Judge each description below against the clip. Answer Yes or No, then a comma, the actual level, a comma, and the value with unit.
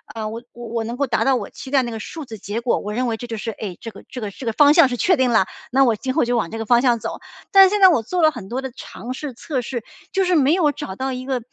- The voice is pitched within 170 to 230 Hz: No, very high, 250 Hz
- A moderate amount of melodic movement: Yes, average, 3.8 semitones